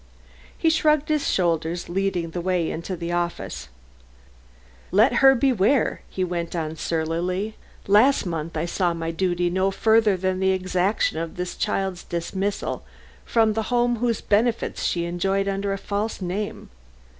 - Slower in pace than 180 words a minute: Yes, average, 150 wpm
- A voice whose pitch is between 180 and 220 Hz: Yes, medium, 185 Hz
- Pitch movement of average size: Yes, average, 3.8 semitones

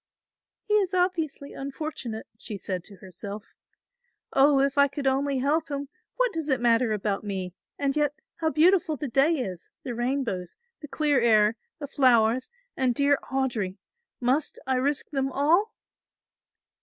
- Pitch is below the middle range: No, very high, 270 Hz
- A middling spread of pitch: Yes, average, 4.4 semitones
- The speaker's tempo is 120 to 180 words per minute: Yes, average, 155 wpm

